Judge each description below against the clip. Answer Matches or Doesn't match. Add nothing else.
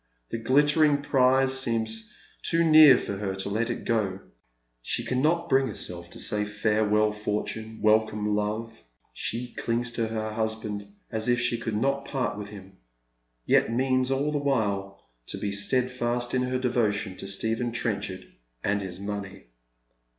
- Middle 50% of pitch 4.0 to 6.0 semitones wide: Doesn't match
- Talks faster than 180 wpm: Doesn't match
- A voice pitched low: Matches